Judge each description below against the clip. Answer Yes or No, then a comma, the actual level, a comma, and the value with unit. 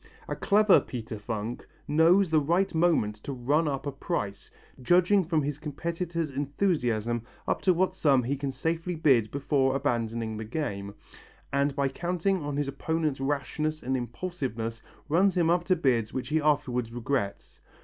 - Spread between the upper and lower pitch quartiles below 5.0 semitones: No, wide, 5.4 semitones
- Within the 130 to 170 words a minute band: Yes, average, 160 wpm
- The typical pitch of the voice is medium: Yes, medium, 145 Hz